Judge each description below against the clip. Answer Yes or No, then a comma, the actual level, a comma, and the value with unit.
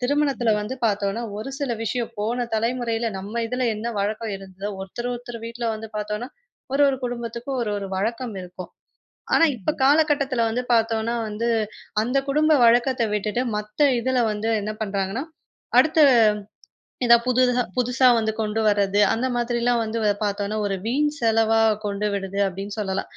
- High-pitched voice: Yes, high, 230 Hz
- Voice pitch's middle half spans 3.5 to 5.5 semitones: No, average, 2.9 semitones